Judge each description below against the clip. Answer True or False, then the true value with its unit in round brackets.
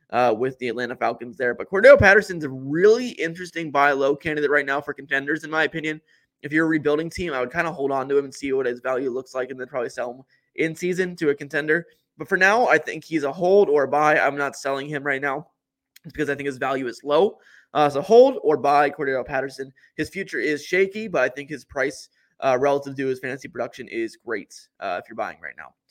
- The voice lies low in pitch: False (145 Hz)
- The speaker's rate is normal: False (250 wpm)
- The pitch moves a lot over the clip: False (3.0 semitones)